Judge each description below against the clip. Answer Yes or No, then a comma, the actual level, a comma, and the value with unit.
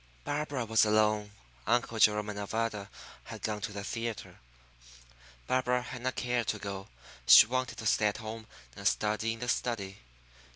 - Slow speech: No, average, 165 wpm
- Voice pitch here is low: Yes, low, 110 Hz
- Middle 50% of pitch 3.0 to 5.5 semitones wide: No, narrow, 2.5 semitones